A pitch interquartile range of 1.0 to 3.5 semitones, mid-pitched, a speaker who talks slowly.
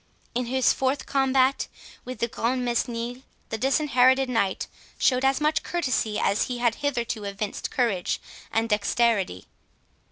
No: narrow, 2.6 semitones; high, 245 Hz; slow, 130 wpm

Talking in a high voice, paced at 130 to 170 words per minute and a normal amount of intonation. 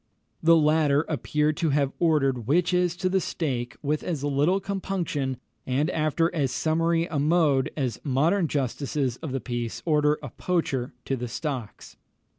No: medium, 150 Hz; average, 155 wpm; average, 3.7 semitones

